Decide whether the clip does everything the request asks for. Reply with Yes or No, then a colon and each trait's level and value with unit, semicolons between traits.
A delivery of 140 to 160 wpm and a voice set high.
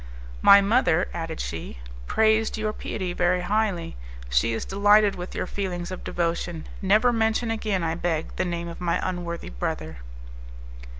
No: average, 155 wpm; medium, 180 Hz